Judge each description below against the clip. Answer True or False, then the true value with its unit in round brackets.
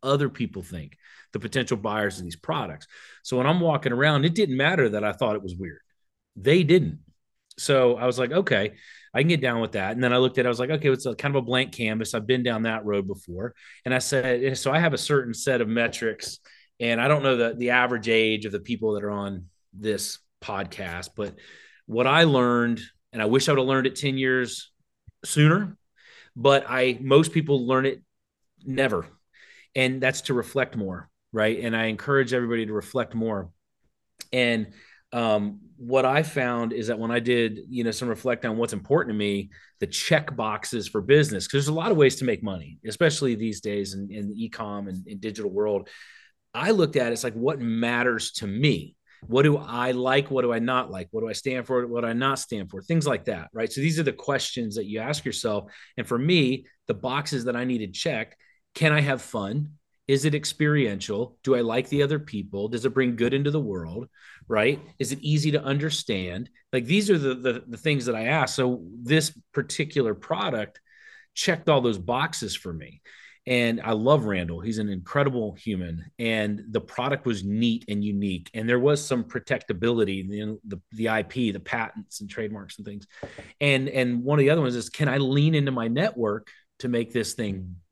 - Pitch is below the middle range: True (125 Hz)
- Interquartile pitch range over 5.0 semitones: False (4.1 semitones)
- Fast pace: True (215 wpm)